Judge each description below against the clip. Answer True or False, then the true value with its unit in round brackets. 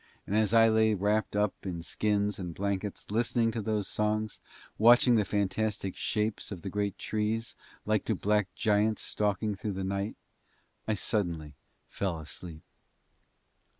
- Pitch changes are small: True (1.9 semitones)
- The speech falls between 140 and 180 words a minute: True (150 wpm)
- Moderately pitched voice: False (105 Hz)